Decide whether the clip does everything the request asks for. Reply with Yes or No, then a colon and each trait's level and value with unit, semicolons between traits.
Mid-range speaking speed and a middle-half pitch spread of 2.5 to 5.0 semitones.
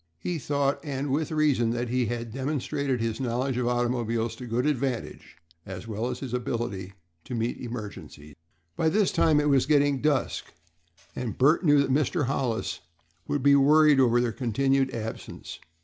Yes: average, 170 wpm; average, 3.2 semitones